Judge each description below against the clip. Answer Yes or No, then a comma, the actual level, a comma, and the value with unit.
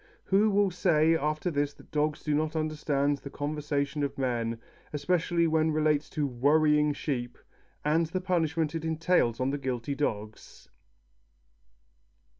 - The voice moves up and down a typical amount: No, narrow, 2.3 semitones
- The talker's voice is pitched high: No, medium, 150 Hz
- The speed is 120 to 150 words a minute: Yes, average, 145 wpm